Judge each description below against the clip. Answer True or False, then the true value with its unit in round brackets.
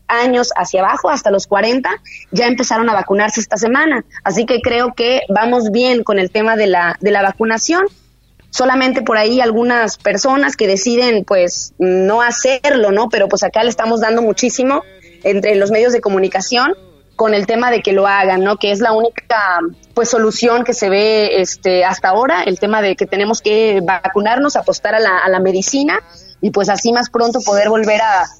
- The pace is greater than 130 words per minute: True (190 wpm)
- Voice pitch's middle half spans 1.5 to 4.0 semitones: True (3.3 semitones)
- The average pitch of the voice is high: True (220 Hz)